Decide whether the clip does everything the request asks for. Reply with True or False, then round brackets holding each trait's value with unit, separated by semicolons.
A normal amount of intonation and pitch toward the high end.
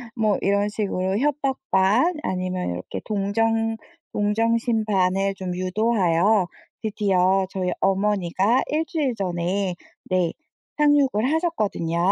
True (3.5 semitones; 200 Hz)